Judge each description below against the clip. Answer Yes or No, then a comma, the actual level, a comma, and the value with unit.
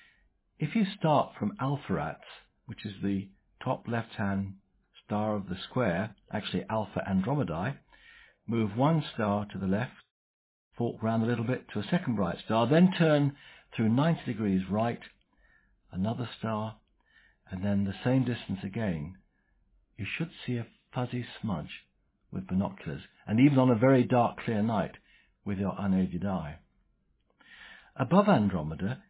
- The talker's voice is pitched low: Yes, low, 110 Hz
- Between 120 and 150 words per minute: Yes, average, 145 wpm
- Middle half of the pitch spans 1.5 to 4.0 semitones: No, average, 4.6 semitones